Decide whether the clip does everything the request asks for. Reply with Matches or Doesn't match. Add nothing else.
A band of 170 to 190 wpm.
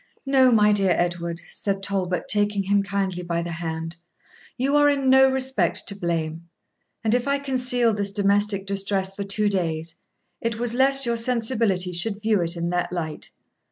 Matches